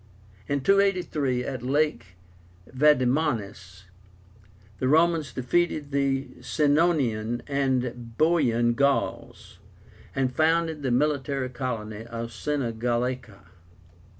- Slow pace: Yes, slow, 90 wpm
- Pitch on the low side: Yes, low, 130 Hz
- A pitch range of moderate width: Yes, average, 3.9 semitones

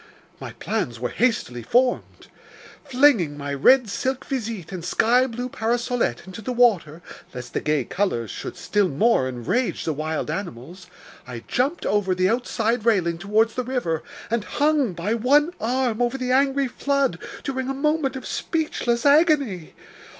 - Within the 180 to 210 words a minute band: No, average, 155 wpm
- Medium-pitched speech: No, high, 230 Hz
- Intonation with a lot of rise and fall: Yes, wide, 7.0 semitones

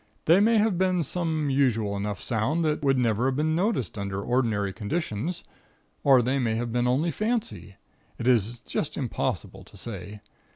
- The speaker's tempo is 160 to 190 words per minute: Yes, average, 170 wpm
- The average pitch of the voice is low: Yes, low, 130 Hz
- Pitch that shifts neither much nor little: No, wide, 6.9 semitones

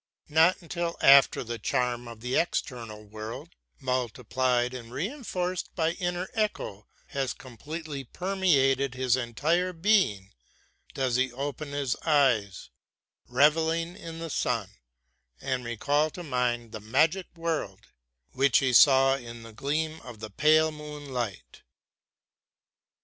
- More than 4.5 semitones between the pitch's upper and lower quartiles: Yes, average, 5.0 semitones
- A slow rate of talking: Yes, slow, 125 wpm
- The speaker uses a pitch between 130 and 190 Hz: Yes, low, 135 Hz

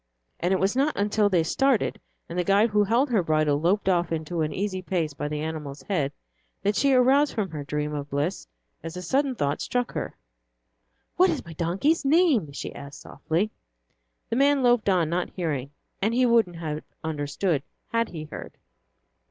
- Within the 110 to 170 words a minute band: No, average, 185 wpm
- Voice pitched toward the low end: No, medium, 180 Hz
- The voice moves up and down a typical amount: No, wide, 7.0 semitones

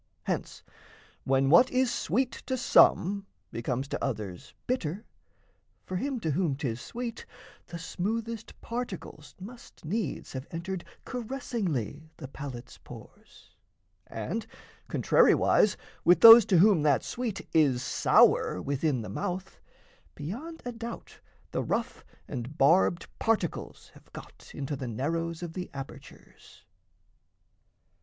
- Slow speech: Yes, slow, 120 wpm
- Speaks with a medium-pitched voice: Yes, medium, 170 Hz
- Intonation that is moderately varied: No, wide, 8.4 semitones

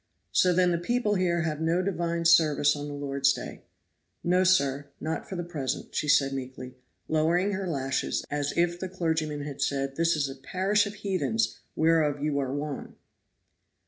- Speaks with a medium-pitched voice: Yes, medium, 160 Hz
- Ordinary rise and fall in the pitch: Yes, average, 3.9 semitones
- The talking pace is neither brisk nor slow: Yes, average, 175 wpm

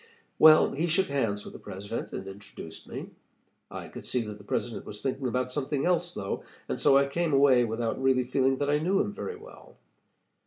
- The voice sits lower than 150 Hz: Yes, low, 135 Hz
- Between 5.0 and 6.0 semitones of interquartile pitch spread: Yes, wide, 5.4 semitones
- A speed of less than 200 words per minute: No, fast, 205 wpm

